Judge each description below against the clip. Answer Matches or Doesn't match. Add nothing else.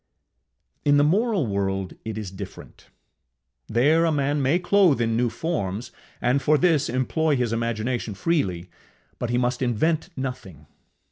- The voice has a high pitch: Doesn't match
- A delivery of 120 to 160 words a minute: Matches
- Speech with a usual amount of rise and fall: Doesn't match